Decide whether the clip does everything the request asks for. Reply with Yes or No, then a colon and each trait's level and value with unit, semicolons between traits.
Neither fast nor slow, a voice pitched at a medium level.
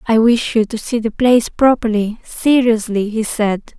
No: average, 175 wpm; high, 225 Hz